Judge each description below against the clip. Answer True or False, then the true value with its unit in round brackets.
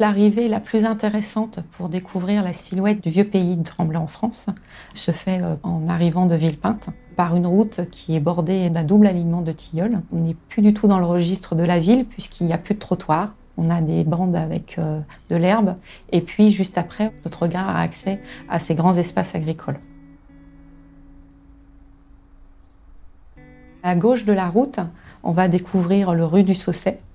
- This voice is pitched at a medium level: True (175 Hz)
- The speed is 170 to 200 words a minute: True (180 wpm)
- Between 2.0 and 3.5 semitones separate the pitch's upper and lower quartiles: True (3.2 semitones)